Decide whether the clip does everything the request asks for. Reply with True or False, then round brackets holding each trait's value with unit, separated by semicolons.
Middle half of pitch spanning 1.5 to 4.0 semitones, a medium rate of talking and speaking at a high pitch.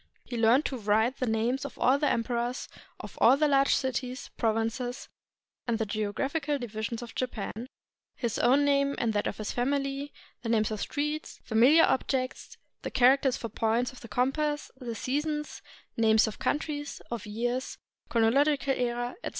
True (3.6 semitones; 170 wpm; 250 Hz)